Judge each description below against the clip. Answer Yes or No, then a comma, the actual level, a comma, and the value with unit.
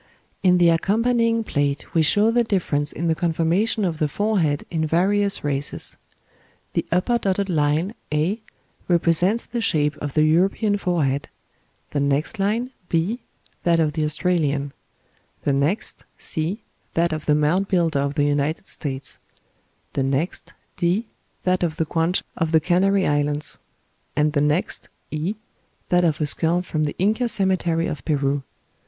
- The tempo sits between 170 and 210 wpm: No, average, 155 wpm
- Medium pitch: Yes, medium, 165 Hz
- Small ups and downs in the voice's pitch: No, average, 4.5 semitones